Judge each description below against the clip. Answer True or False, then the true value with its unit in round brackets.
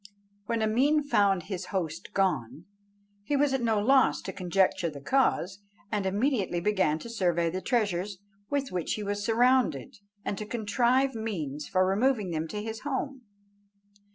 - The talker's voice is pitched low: False (205 Hz)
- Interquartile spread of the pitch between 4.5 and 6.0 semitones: True (5.2 semitones)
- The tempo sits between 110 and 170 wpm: True (155 wpm)